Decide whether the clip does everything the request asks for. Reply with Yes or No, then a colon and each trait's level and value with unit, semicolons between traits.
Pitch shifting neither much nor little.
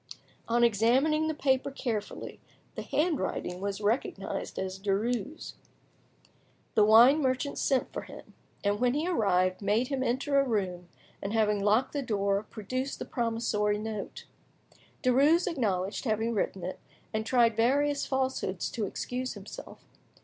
Yes: average, 4.5 semitones